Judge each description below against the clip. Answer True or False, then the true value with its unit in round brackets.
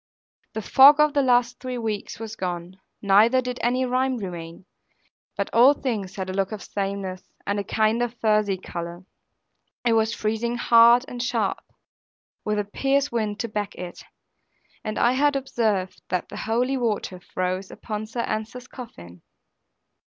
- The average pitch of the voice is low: False (220 Hz)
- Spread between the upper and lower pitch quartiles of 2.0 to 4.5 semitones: True (4.0 semitones)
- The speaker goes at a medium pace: True (160 wpm)